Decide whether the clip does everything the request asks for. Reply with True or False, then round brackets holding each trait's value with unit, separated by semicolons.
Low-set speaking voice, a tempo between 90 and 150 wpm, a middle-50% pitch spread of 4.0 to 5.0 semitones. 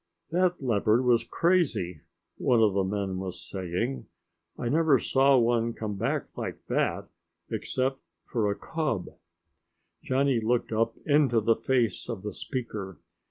True (115 Hz; 140 wpm; 4.5 semitones)